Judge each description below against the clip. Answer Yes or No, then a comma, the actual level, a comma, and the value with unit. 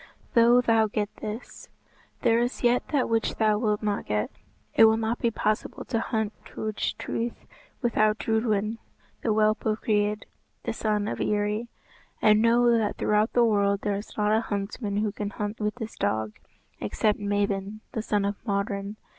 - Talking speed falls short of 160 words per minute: No, average, 170 wpm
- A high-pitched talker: Yes, high, 215 Hz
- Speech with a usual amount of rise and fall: No, narrow, 1.7 semitones